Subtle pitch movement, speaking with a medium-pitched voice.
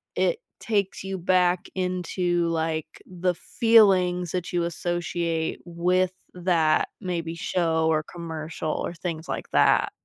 Yes: narrow, 1.8 semitones; medium, 175 Hz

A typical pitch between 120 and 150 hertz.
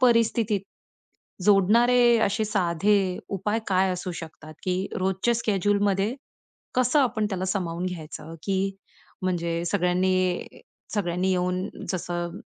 No: high, 190 Hz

